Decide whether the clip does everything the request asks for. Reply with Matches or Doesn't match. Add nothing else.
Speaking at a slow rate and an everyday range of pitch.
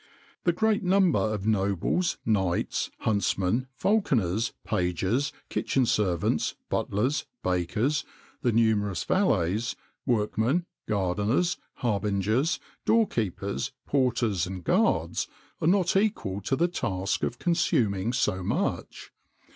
Doesn't match